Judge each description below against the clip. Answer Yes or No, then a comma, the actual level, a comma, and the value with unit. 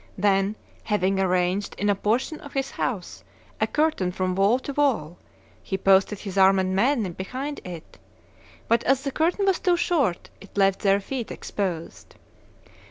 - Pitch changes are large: Yes, wide, 6.1 semitones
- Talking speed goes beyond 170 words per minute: No, average, 160 wpm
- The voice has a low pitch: No, high, 200 Hz